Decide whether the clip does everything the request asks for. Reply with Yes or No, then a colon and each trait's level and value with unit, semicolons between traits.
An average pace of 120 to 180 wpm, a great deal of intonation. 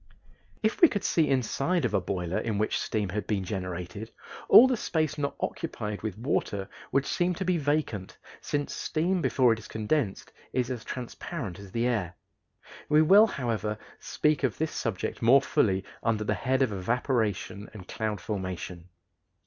Yes: average, 170 wpm; wide, 6.5 semitones